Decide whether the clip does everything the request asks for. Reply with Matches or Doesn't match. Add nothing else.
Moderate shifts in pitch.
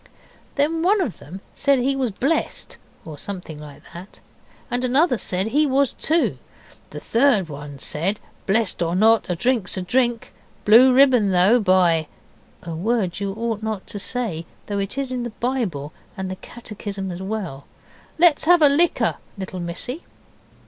Doesn't match